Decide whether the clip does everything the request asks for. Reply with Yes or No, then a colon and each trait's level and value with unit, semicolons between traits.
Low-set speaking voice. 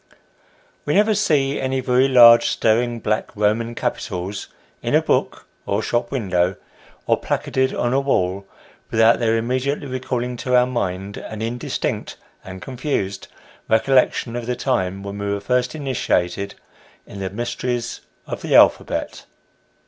Yes: low, 120 Hz